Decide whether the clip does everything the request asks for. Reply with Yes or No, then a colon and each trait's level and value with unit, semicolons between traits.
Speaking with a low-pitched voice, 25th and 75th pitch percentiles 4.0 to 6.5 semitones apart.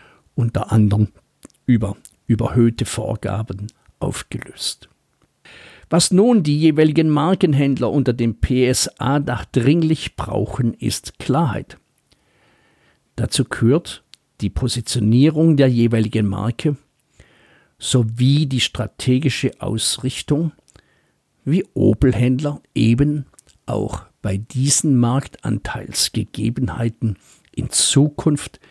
Yes: low, 125 Hz; average, 4.4 semitones